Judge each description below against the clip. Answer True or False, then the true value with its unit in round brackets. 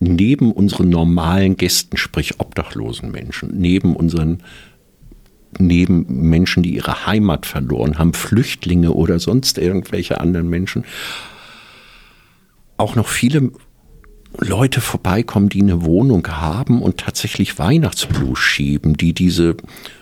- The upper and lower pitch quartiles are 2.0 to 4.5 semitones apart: True (3.3 semitones)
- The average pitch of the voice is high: False (90 Hz)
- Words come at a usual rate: False (110 wpm)